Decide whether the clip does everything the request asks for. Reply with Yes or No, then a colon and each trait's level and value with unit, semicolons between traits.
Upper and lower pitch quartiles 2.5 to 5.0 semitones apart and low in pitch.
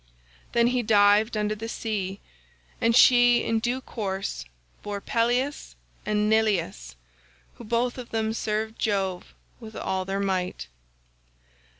No: average, 2.8 semitones; high, 215 Hz